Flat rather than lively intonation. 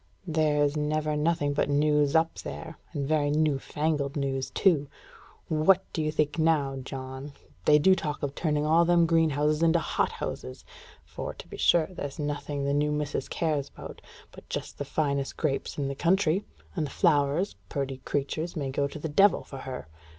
Yes: narrow, 2.2 semitones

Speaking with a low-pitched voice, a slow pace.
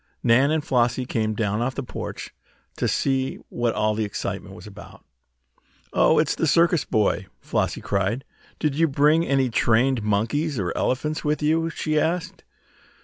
No: low, 130 Hz; average, 160 wpm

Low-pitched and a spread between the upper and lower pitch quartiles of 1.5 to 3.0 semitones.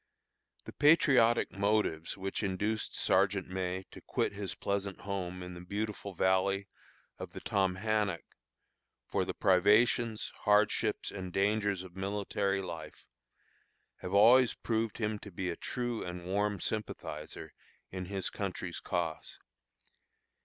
Yes: low, 100 Hz; narrow, 2.4 semitones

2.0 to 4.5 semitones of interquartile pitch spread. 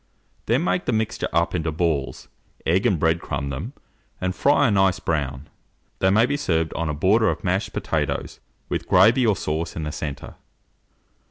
No: average, 5.2 semitones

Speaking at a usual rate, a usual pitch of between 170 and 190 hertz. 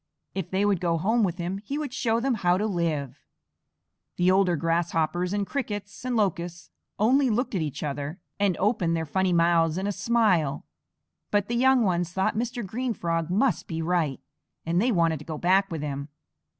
Yes: average, 190 wpm; medium, 185 Hz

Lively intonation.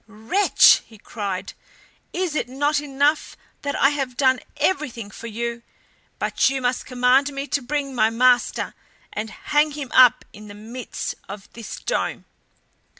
No: average, 3.9 semitones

